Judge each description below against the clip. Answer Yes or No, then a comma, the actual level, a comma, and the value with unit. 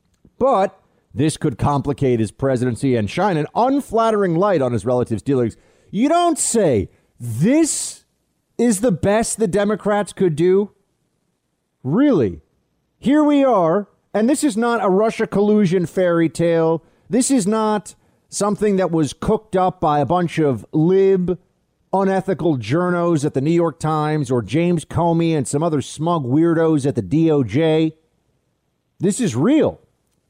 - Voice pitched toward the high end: No, medium, 170 Hz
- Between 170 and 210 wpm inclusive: No, average, 145 wpm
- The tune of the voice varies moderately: No, wide, 5.8 semitones